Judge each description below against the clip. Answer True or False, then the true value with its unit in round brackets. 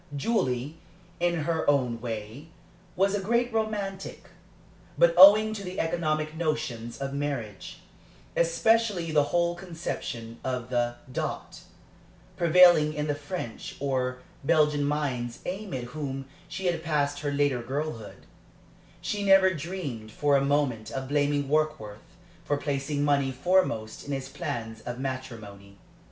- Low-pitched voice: False (145 Hz)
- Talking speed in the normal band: False (130 wpm)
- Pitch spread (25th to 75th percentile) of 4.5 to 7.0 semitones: True (5.2 semitones)